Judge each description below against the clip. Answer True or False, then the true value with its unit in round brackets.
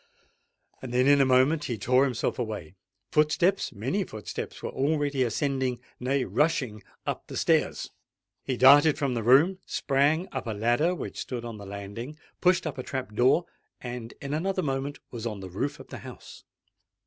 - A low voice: True (130 Hz)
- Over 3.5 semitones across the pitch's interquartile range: True (4.0 semitones)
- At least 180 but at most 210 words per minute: False (150 wpm)